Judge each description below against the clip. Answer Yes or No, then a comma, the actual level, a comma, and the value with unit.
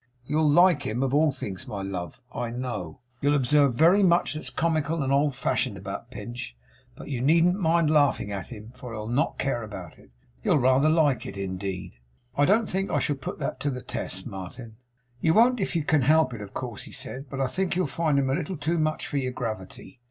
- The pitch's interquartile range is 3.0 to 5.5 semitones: Yes, average, 5.1 semitones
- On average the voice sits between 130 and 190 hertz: Yes, low, 135 Hz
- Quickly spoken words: Yes, fast, 220 wpm